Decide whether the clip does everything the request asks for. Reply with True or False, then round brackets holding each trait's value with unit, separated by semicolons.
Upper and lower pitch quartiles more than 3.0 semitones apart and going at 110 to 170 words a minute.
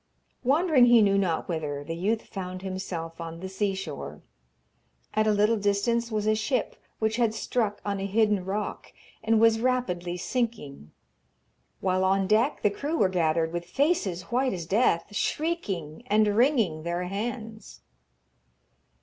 True (4.3 semitones; 150 wpm)